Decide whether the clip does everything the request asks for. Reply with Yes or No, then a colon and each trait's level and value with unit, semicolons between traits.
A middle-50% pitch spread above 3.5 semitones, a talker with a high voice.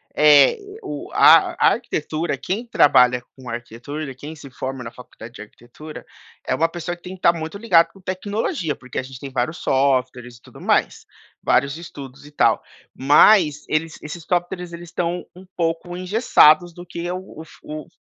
No: average, 4.7 semitones; medium, 155 Hz